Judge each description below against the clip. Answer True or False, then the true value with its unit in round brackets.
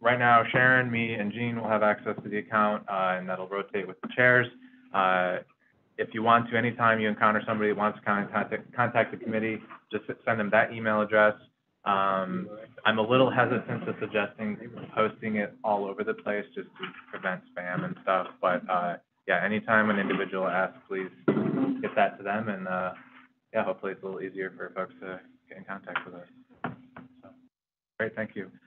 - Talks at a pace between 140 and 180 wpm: False (195 wpm)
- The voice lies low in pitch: True (110 Hz)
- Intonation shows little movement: False (3.1 semitones)